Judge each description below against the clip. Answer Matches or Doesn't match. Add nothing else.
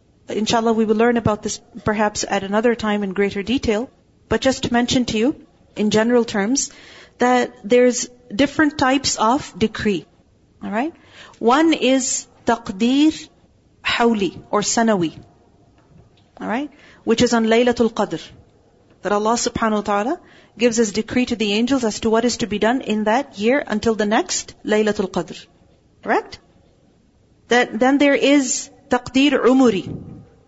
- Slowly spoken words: Doesn't match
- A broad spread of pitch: Doesn't match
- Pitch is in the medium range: Doesn't match